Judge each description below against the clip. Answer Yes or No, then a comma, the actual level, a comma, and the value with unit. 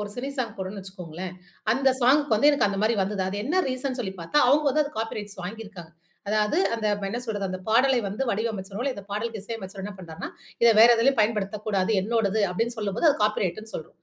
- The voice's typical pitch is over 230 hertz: No, high, 215 Hz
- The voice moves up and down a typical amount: Yes, average, 3.5 semitones